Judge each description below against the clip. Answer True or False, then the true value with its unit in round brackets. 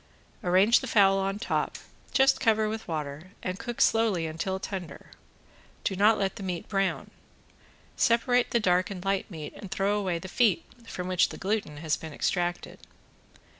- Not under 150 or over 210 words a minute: True (170 wpm)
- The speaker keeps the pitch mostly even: False (3.4 semitones)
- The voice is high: True (195 Hz)